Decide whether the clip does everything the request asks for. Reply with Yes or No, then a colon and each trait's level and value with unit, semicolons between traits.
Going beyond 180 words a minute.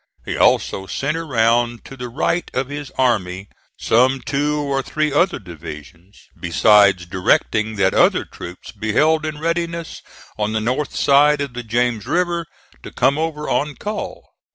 No: average, 155 wpm